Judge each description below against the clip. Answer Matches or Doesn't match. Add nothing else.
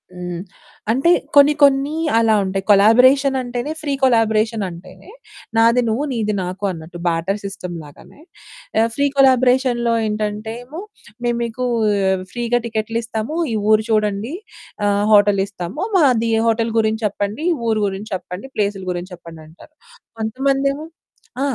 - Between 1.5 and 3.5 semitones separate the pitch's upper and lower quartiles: Doesn't match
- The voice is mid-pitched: Doesn't match